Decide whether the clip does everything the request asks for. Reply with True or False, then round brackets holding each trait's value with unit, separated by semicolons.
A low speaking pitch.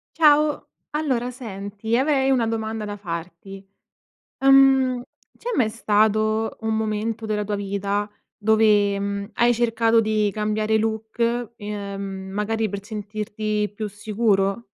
False (215 Hz)